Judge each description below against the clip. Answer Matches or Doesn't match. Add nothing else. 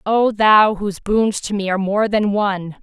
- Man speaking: Doesn't match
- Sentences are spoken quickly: Matches